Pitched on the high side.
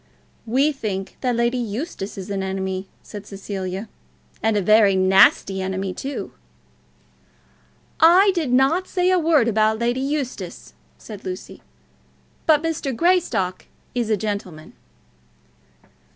Yes: high, 220 Hz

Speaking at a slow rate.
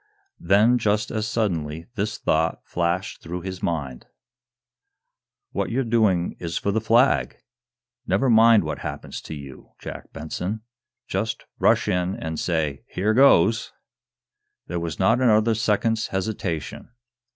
Yes: slow, 130 wpm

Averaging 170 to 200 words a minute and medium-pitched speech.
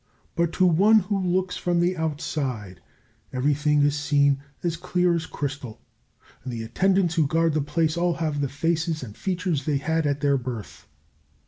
Yes: average, 175 wpm; medium, 155 Hz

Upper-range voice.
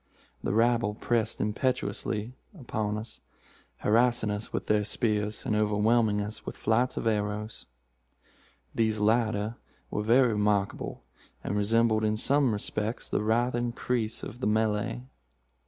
No: low, 110 Hz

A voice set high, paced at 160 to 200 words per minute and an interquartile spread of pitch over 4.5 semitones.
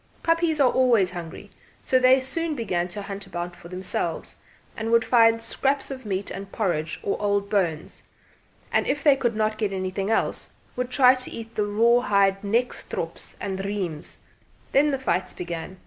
Yes: high, 210 Hz; average, 175 wpm; average, 5.0 semitones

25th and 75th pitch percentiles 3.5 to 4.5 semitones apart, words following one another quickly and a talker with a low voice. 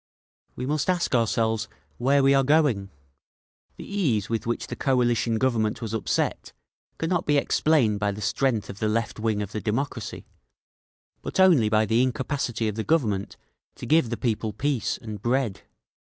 No: average, 4.2 semitones; average, 165 wpm; low, 115 Hz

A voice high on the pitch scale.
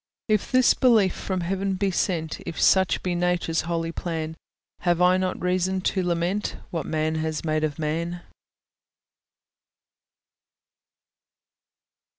No: medium, 175 Hz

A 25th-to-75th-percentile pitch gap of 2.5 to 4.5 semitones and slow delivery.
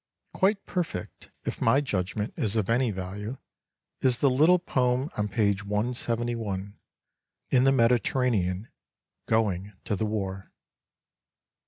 Yes: average, 3.9 semitones; slow, 125 wpm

